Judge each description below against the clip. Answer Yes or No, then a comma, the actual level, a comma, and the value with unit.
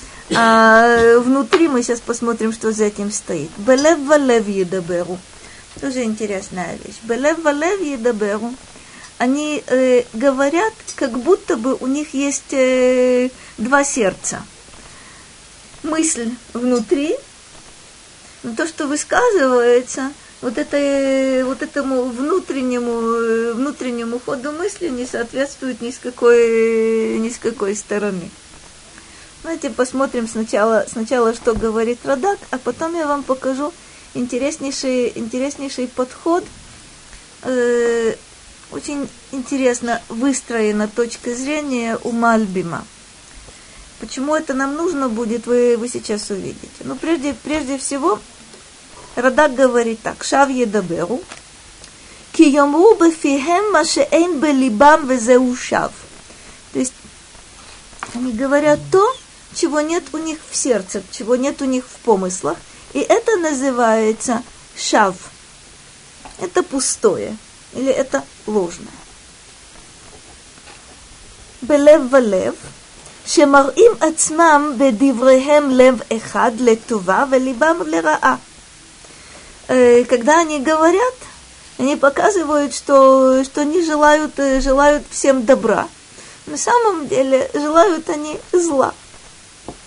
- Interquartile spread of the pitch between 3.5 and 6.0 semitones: Yes, average, 4.0 semitones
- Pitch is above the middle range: Yes, very high, 265 Hz